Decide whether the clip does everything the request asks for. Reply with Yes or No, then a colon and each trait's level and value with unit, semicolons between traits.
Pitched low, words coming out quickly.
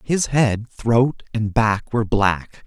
No: low, 115 Hz; average, 160 wpm